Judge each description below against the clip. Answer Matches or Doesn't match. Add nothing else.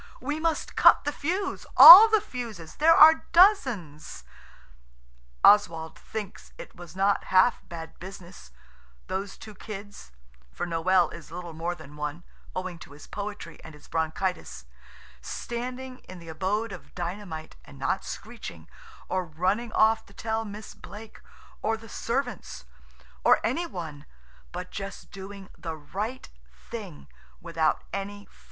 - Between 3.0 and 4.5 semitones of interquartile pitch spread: Doesn't match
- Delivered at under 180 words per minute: Matches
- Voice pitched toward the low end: Doesn't match